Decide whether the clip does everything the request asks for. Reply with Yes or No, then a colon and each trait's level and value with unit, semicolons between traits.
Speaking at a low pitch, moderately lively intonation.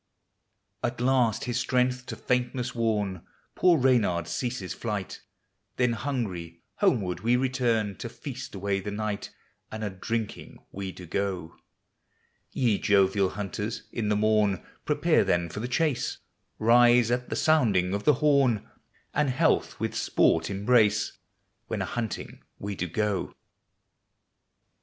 Yes: low, 110 Hz; average, 4.0 semitones